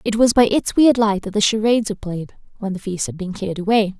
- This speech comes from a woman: Yes, female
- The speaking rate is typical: No, fast, 270 wpm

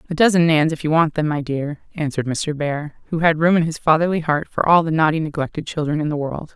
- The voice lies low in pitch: No, medium, 155 Hz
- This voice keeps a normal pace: No, fast, 255 wpm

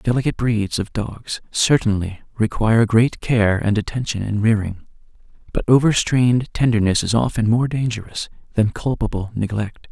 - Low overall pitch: Yes, low, 110 Hz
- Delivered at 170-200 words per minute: No, slow, 135 wpm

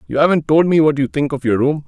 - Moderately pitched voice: Yes, medium, 150 Hz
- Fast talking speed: Yes, fast, 320 wpm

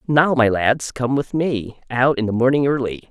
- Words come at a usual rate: No, fast, 210 wpm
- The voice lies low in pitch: Yes, low, 125 Hz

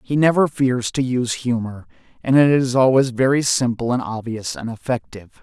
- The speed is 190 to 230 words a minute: No, average, 175 wpm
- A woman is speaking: No, male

